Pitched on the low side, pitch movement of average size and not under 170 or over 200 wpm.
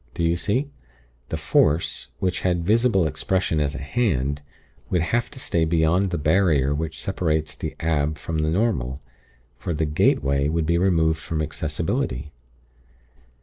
No: very low, 80 Hz; average, 3.4 semitones; average, 150 wpm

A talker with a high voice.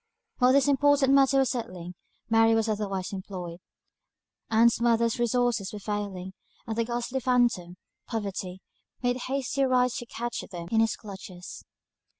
Yes: high, 225 Hz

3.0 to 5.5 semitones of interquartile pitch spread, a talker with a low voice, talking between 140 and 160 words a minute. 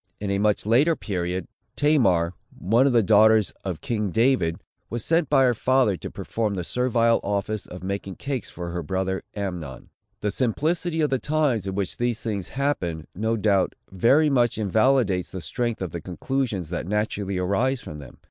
No: average, 5.2 semitones; low, 105 Hz; average, 180 wpm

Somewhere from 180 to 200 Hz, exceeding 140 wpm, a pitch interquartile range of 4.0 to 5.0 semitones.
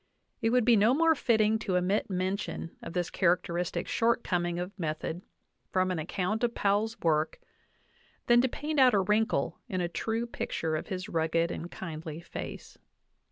Yes: medium, 185 Hz; average, 175 wpm; average, 4.6 semitones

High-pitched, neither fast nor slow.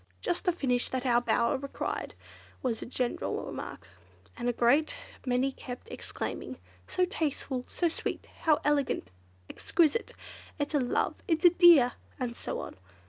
Yes: very high, 275 Hz; average, 150 wpm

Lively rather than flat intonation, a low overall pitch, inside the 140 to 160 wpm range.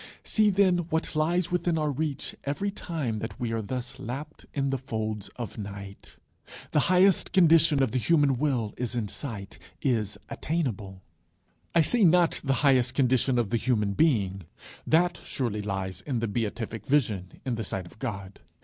No: wide, 6.4 semitones; low, 130 Hz; average, 170 wpm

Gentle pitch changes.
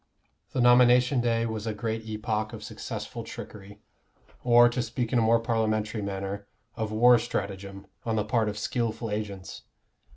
Yes: narrow, 2.1 semitones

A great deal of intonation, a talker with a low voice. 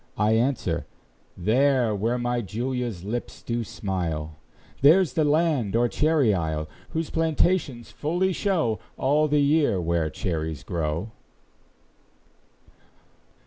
Yes: wide, 7.8 semitones; low, 120 Hz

